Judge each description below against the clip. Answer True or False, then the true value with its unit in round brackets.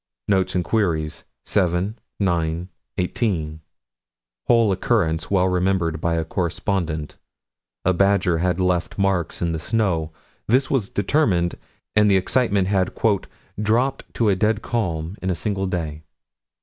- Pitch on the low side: True (95 Hz)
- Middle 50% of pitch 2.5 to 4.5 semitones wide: True (3.4 semitones)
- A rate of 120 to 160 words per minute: True (135 wpm)